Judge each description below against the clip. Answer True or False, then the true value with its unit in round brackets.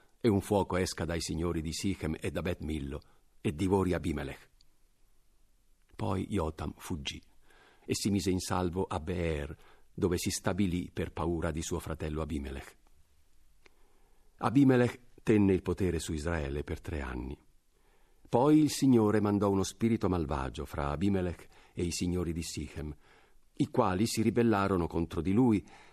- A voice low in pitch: True (90 Hz)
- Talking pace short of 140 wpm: False (145 wpm)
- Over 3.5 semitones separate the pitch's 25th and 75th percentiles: True (4.1 semitones)